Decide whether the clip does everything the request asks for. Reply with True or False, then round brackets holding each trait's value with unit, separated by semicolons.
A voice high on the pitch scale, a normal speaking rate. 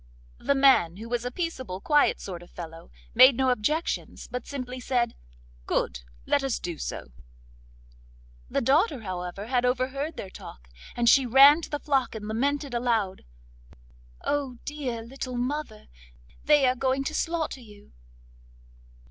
True (250 Hz; 150 wpm)